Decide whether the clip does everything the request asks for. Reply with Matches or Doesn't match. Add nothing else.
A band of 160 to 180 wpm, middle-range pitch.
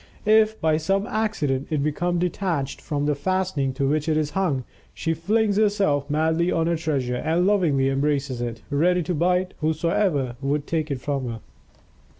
Matches